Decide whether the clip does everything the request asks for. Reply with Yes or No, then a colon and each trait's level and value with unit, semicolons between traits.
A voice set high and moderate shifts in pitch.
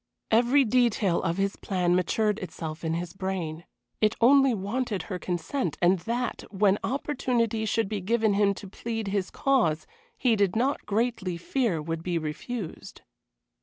Yes: high, 200 Hz; average, 4.7 semitones